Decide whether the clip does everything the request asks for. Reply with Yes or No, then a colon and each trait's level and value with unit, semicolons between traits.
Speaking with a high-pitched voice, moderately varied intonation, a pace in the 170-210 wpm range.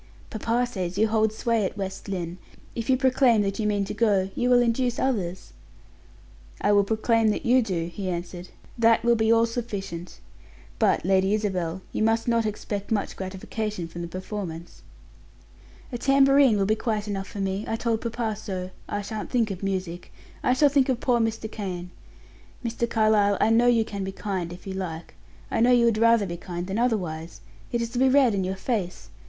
Yes: high, 210 Hz; average, 3.5 semitones; average, 200 wpm